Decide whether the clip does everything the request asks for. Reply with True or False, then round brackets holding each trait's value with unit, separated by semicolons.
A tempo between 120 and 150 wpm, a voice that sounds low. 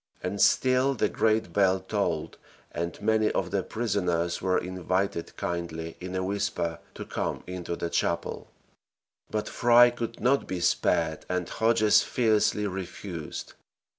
True (135 wpm; 95 Hz)